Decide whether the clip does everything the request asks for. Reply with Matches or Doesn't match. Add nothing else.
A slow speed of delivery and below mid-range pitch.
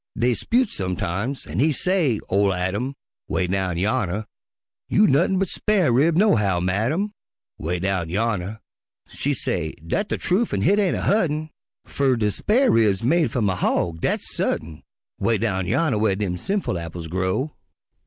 Doesn't match